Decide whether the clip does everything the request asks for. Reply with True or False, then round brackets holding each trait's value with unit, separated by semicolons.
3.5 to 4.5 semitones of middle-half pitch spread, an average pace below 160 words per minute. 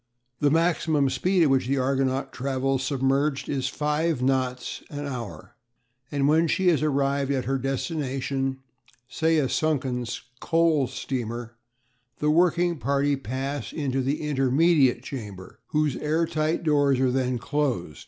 False (2.6 semitones; 140 wpm)